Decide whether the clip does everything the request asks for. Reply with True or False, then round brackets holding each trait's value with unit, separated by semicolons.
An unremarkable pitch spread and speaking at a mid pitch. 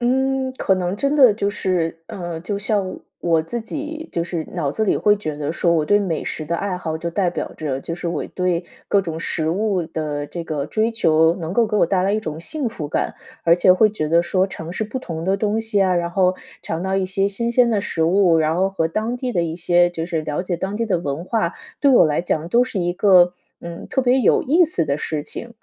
True (4.3 semitones; 180 Hz)